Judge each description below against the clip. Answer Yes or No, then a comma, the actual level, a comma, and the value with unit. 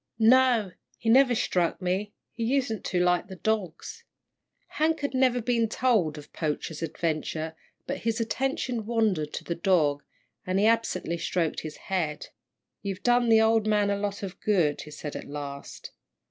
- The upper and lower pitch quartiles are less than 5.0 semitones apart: No, wide, 5.5 semitones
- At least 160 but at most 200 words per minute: Yes, average, 165 wpm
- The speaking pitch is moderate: No, high, 205 Hz